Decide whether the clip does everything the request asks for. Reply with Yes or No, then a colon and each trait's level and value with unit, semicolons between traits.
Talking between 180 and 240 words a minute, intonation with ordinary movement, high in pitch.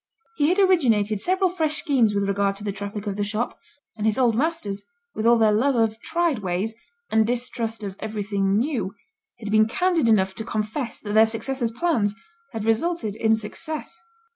Yes: average, 185 wpm; average, 4.7 semitones; high, 225 Hz